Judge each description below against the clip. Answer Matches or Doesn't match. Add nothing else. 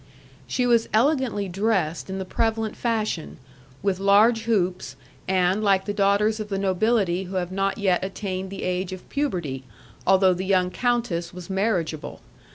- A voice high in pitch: Matches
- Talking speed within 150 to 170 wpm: Matches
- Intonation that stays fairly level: Doesn't match